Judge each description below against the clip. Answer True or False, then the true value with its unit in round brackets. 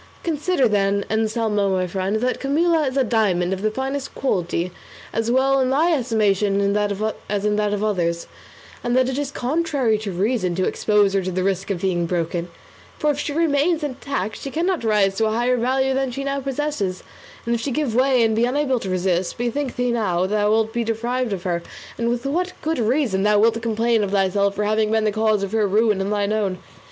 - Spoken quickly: True (215 wpm)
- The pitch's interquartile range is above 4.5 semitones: True (4.9 semitones)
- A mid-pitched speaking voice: False (220 Hz)